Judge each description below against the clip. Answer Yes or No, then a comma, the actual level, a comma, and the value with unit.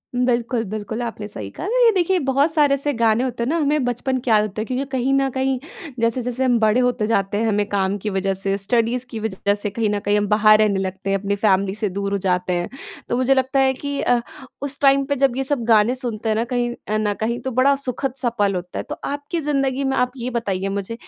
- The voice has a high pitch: Yes, high, 235 Hz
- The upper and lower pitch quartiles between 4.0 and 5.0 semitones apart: Yes, average, 4.3 semitones